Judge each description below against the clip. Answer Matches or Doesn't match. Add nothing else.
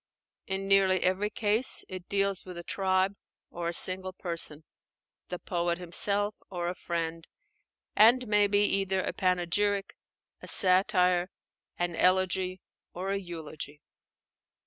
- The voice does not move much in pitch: Matches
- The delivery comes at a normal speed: Doesn't match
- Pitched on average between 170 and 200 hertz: Matches